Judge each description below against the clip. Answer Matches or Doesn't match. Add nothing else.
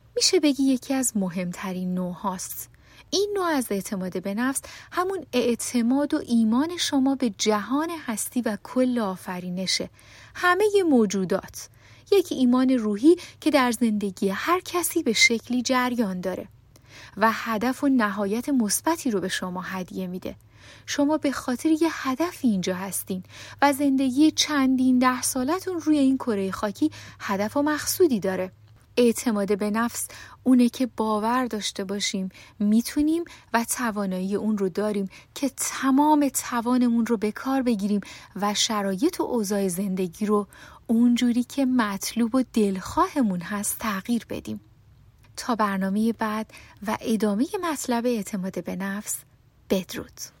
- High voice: Matches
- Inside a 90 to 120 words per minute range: Doesn't match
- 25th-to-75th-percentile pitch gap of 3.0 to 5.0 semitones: Doesn't match